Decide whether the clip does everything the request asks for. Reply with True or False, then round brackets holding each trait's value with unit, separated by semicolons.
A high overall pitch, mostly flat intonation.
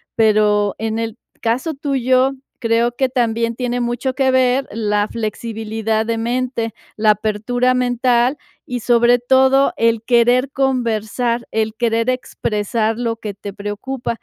True (235 Hz; 2.3 semitones)